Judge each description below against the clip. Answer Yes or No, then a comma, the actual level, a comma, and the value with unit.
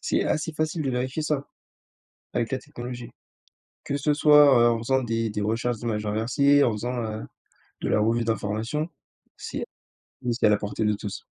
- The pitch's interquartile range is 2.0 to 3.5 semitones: No, average, 4.3 semitones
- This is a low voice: Yes, low, 120 Hz